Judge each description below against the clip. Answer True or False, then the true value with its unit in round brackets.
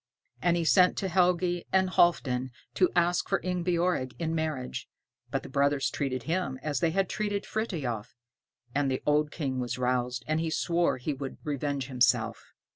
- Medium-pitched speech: True (150 Hz)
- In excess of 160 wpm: True (170 wpm)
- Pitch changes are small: False (5.2 semitones)